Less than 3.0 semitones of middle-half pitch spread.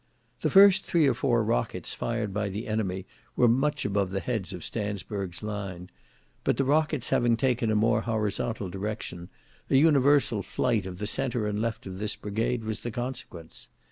No: average, 3.8 semitones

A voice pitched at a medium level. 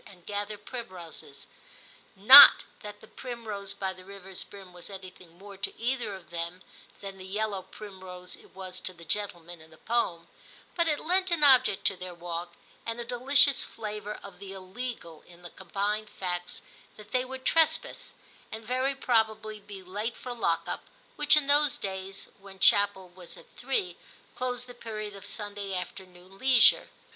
No: high, 200 Hz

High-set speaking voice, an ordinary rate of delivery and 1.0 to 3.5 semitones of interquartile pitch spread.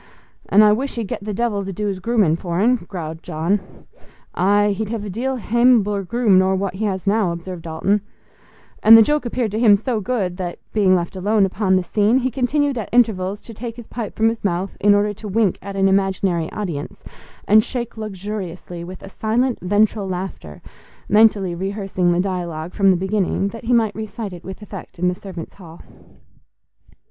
Yes: high, 200 Hz; average, 190 wpm; average, 3.0 semitones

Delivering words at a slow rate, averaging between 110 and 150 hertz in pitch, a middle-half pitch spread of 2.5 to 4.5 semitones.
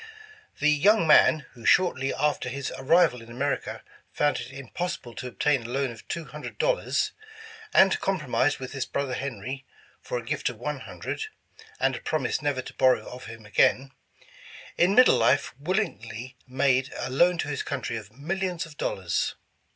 No: average, 180 wpm; medium, 140 Hz; average, 4.2 semitones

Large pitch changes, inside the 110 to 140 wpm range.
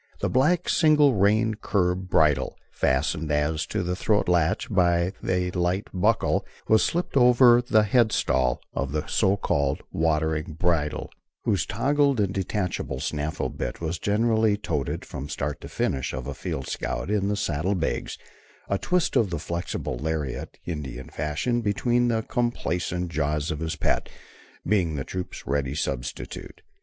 No: wide, 6.1 semitones; average, 155 wpm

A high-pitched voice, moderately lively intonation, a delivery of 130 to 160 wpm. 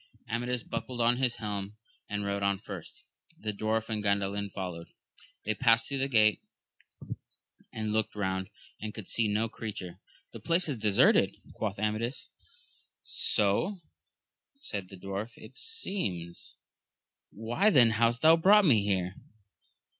No: low, 110 Hz; average, 3.1 semitones; average, 140 wpm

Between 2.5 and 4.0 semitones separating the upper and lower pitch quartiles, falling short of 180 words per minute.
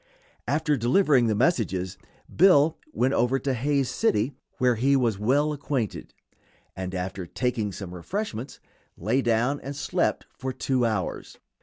No: average, 4.7 semitones; average, 140 wpm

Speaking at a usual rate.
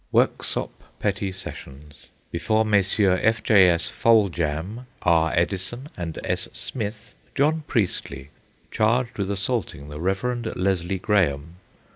No: slow, 115 wpm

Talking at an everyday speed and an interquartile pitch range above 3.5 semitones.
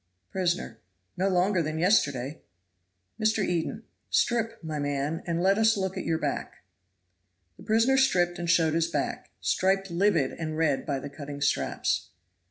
Yes: average, 155 wpm; average, 3.9 semitones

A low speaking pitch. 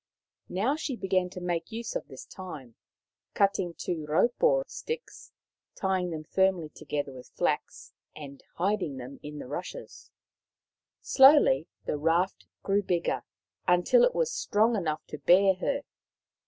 No: medium, 180 Hz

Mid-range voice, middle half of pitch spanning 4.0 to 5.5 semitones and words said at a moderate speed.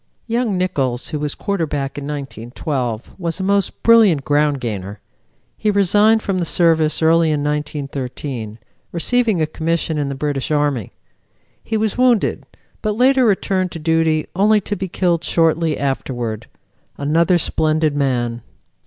Yes: medium, 155 Hz; average, 5.2 semitones; average, 145 wpm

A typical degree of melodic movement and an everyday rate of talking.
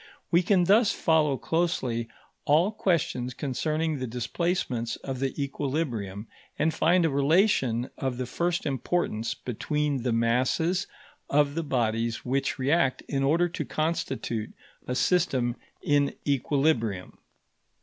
No: average, 5.0 semitones; slow, 125 wpm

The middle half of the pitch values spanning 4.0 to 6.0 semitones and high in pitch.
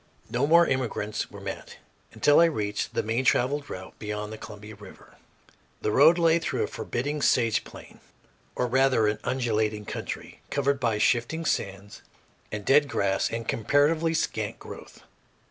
No: average, 5.3 semitones; low, 120 Hz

